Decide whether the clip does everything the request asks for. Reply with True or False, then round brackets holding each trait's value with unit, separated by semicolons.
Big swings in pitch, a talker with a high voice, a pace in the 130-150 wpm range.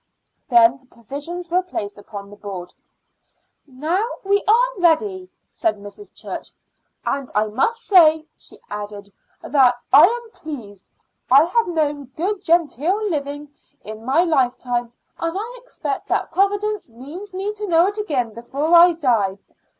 True (7.6 semitones; 310 Hz; 145 wpm)